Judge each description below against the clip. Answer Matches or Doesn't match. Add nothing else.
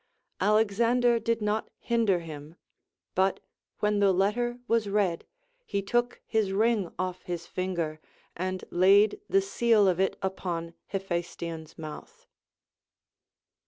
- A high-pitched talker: Matches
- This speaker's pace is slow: Matches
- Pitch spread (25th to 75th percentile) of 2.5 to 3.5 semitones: Doesn't match